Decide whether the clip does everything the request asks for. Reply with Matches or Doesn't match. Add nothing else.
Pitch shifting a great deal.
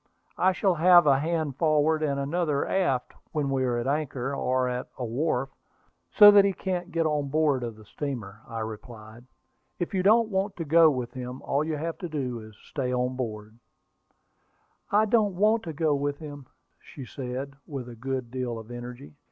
Doesn't match